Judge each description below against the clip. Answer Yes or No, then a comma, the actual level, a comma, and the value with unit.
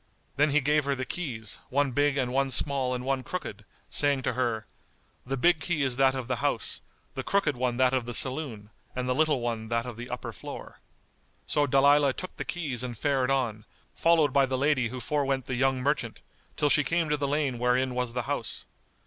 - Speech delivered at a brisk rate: Yes, fast, 215 wpm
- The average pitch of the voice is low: Yes, low, 130 Hz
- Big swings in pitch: No, average, 2.7 semitones